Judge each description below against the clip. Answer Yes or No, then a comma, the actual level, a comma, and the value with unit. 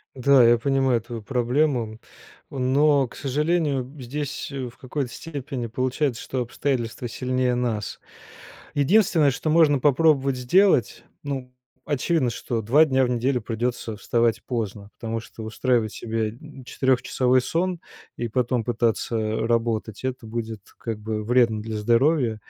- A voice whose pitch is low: Yes, low, 125 Hz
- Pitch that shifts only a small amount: No, average, 3.2 semitones